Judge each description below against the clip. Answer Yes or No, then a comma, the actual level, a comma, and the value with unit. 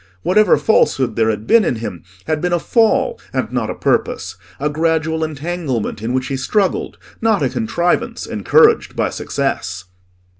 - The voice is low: No, medium, 155 Hz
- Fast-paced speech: No, average, 160 wpm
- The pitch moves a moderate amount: No, wide, 6.7 semitones